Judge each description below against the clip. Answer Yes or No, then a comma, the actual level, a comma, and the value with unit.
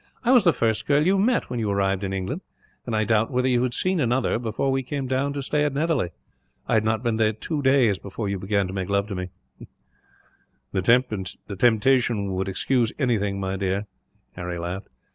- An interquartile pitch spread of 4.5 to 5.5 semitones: Yes, average, 5.2 semitones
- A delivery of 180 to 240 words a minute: Yes, fast, 205 wpm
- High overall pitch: No, low, 110 Hz